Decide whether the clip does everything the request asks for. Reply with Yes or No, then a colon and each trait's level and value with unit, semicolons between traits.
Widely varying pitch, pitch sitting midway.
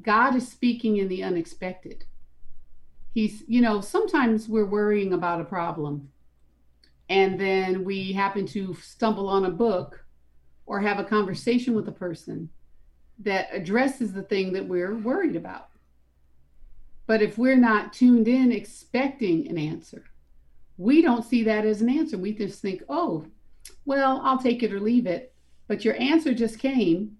No: wide, 5.7 semitones; high, 205 Hz